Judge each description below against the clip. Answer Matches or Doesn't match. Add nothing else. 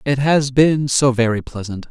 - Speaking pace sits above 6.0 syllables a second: Doesn't match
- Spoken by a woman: Doesn't match